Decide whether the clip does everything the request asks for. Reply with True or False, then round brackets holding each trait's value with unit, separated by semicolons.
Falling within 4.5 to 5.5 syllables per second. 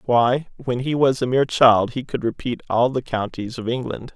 True (5.0 syllables/s)